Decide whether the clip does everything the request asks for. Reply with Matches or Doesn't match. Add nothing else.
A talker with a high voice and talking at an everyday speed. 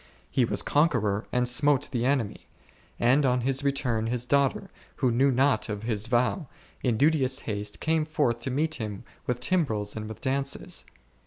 Doesn't match